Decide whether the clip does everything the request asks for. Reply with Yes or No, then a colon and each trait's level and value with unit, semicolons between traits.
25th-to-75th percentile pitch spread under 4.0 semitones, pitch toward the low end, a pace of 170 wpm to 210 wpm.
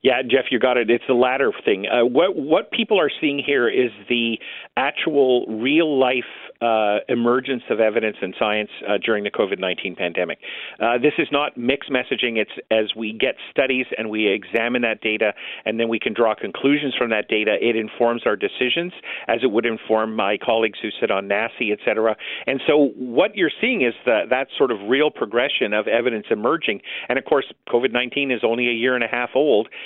Yes: average, 2.9 semitones; low, 120 Hz; fast, 205 wpm